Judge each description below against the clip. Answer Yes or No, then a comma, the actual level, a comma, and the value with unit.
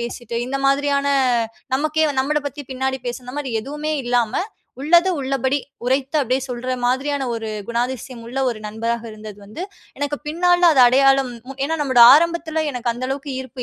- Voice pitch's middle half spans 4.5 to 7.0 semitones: No, average, 3.0 semitones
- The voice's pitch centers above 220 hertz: Yes, very high, 265 Hz